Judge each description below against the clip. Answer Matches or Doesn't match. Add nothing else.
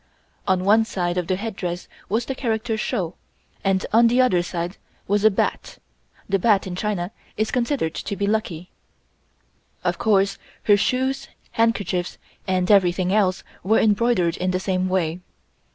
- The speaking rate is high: Doesn't match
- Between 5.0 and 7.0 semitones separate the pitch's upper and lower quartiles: Doesn't match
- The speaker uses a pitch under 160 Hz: Doesn't match